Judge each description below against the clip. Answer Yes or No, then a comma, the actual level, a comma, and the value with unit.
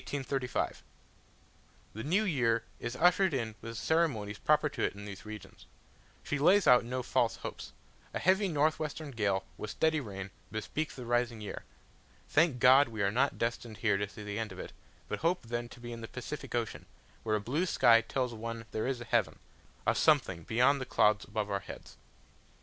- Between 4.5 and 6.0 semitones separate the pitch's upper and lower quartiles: Yes, average, 5.1 semitones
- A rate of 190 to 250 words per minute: Yes, average, 195 wpm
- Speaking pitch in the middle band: No, low, 120 Hz